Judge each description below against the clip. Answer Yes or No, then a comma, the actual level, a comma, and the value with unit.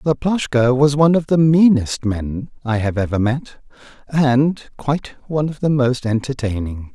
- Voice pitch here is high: No, low, 130 Hz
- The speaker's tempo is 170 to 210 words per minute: No, average, 155 wpm